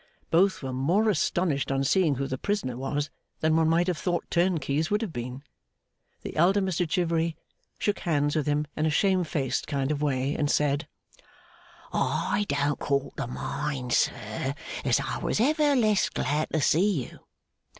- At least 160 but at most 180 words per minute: Yes, average, 170 wpm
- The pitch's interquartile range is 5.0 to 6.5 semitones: No, average, 4.6 semitones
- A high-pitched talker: No, medium, 155 Hz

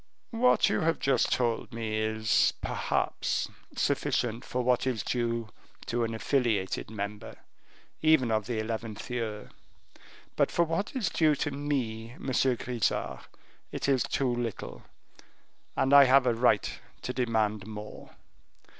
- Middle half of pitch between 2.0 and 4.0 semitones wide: Yes, average, 3.4 semitones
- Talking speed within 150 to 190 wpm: No, slow, 135 wpm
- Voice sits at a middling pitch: No, low, 120 Hz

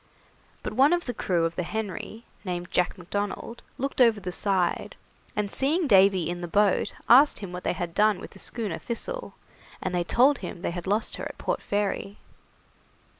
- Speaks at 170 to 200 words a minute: Yes, average, 190 wpm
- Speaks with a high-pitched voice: Yes, high, 200 Hz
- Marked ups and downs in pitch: No, average, 4.6 semitones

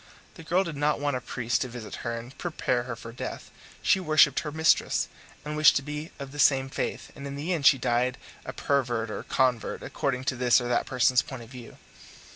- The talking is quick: Yes, fast, 225 wpm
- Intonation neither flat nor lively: Yes, average, 3.4 semitones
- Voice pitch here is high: No, low, 135 Hz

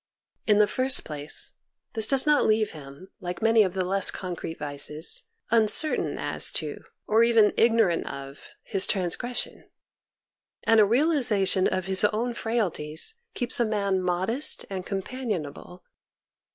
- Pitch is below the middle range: No, high, 205 Hz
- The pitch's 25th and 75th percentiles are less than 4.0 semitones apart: No, average, 4.3 semitones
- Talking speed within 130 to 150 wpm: Yes, average, 140 wpm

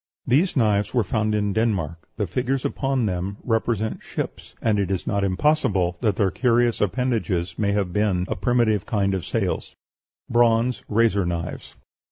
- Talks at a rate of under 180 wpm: Yes, average, 160 wpm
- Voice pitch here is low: Yes, low, 105 Hz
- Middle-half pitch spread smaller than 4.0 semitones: Yes, average, 3.5 semitones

